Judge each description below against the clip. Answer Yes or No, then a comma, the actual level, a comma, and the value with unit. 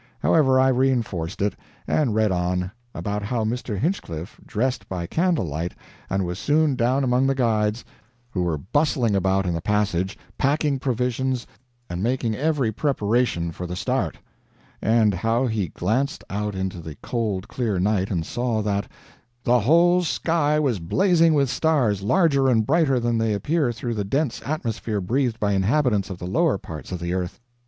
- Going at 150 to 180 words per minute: Yes, average, 170 wpm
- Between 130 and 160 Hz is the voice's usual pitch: No, low, 115 Hz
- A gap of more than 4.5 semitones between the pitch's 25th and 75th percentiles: Yes, wide, 5.6 semitones